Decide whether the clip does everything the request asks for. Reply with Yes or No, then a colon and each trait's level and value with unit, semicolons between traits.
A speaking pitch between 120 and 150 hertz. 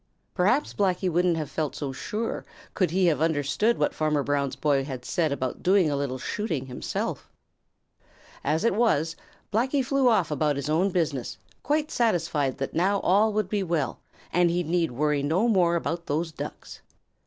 No: medium, 165 Hz